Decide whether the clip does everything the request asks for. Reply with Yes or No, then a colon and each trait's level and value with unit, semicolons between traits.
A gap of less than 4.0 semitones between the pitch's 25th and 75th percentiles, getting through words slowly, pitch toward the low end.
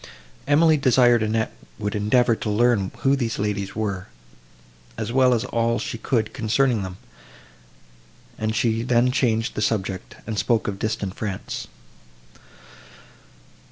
Yes: average, 2.8 semitones; slow, 130 wpm; low, 115 Hz